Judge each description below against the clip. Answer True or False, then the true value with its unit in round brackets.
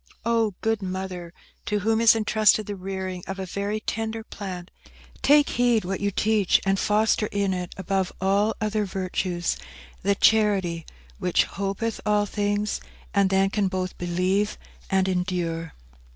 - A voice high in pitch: True (195 Hz)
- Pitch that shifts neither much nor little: False (2.3 semitones)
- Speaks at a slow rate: False (150 wpm)